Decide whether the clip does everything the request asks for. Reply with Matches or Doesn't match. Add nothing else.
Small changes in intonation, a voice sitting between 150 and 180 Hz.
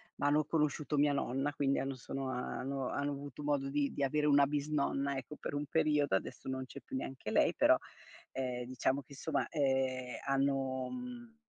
Doesn't match